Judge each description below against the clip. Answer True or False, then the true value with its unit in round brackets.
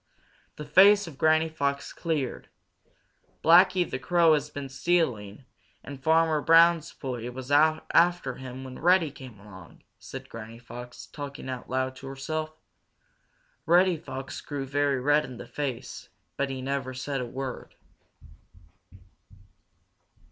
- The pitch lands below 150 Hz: True (140 Hz)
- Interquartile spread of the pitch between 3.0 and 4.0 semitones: True (3.5 semitones)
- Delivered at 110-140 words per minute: True (135 wpm)